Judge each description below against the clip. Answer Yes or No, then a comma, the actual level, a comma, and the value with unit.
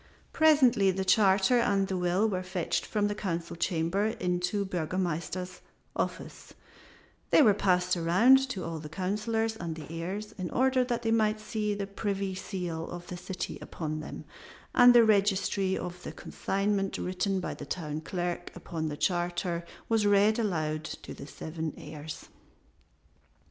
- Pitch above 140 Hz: Yes, high, 190 Hz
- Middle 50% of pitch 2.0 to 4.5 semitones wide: Yes, average, 3.2 semitones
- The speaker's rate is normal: Yes, average, 160 wpm